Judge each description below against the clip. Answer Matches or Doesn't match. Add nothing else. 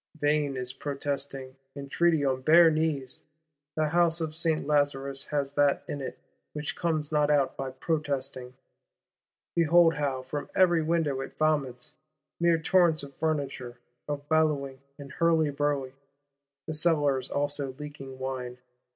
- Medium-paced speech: Doesn't match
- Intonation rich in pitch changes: Doesn't match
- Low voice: Doesn't match